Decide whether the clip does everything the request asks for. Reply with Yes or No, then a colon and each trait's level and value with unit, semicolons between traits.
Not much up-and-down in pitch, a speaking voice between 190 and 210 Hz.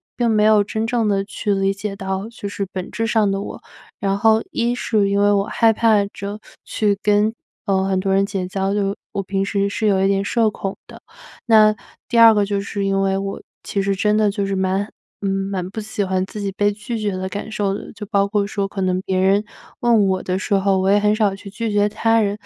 Yes: narrow, 1.5 semitones; high, 200 Hz